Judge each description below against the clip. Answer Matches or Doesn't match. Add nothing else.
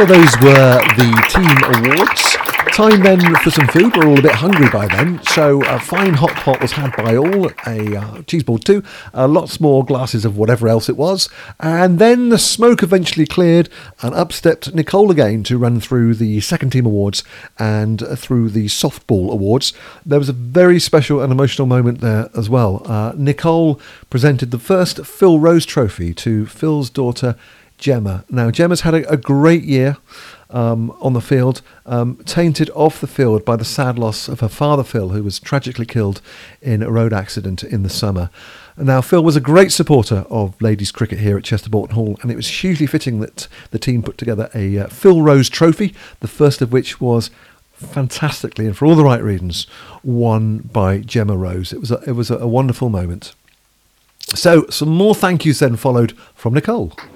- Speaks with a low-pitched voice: Matches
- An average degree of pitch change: Doesn't match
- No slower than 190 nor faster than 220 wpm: Matches